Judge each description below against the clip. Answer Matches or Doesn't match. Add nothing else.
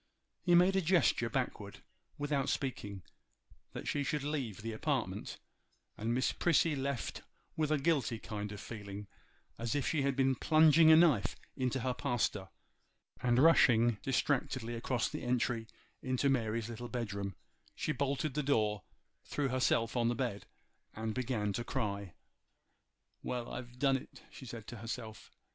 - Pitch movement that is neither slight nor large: Matches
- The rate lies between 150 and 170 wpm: Matches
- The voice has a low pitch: Matches